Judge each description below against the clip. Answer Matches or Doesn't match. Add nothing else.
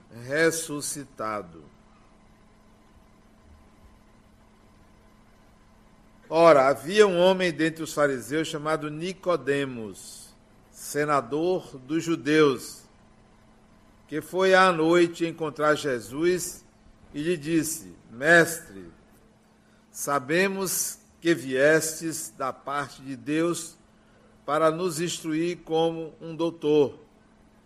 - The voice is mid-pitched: Matches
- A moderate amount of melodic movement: Matches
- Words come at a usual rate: Doesn't match